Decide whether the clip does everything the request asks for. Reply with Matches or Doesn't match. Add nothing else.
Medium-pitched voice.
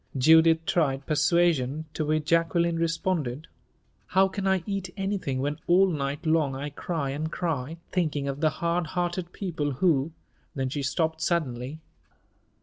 Matches